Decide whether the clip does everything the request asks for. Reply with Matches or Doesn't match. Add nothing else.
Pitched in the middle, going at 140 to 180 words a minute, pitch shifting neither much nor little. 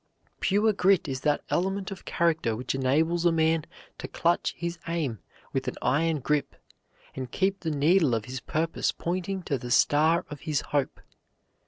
Matches